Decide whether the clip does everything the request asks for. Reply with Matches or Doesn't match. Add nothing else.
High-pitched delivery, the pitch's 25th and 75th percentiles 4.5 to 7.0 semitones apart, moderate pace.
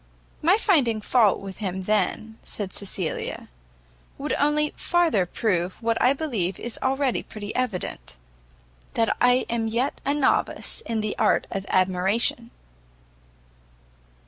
Doesn't match